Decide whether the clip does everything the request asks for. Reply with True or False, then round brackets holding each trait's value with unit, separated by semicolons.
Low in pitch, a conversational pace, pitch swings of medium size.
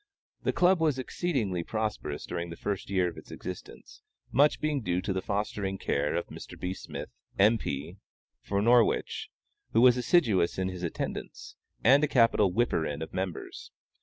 False (100 Hz; 170 wpm; 5.9 semitones)